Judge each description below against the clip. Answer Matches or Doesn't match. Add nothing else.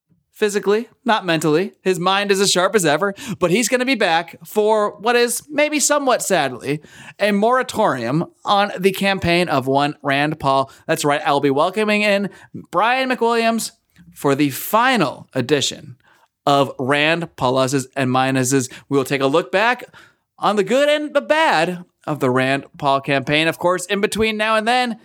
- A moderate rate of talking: Matches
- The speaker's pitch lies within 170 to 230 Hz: Matches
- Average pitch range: Doesn't match